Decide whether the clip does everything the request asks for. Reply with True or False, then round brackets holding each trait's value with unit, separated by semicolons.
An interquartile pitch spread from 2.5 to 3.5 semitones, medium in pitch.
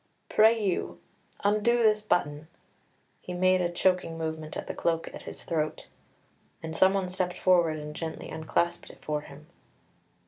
True (3.1 semitones; 175 Hz)